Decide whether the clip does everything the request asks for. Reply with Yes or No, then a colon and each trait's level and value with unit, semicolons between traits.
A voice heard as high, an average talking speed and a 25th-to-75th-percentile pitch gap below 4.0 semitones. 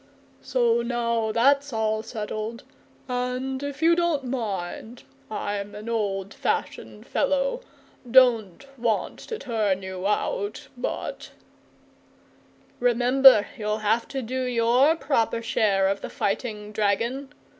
No: high, 230 Hz; slow, 120 wpm; average, 3.6 semitones